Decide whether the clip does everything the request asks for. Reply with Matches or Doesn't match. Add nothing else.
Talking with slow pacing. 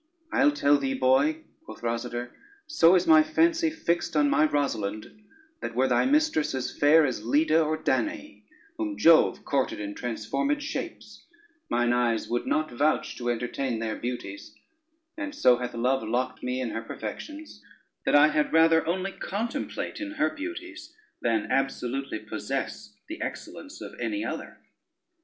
Doesn't match